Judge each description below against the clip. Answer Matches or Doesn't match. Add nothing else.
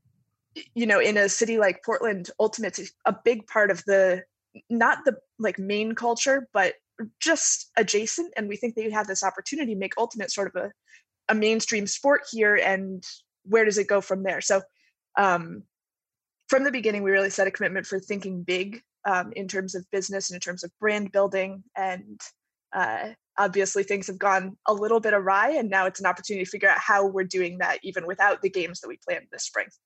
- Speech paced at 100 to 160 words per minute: Doesn't match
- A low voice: Doesn't match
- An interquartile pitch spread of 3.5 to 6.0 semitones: Doesn't match